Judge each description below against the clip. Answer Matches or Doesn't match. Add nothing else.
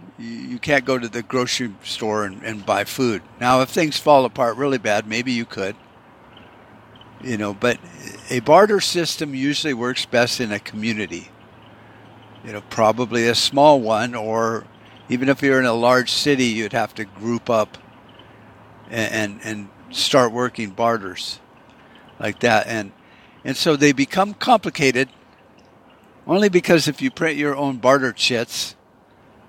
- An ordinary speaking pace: Matches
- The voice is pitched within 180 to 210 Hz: Doesn't match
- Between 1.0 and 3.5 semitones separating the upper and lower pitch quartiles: Doesn't match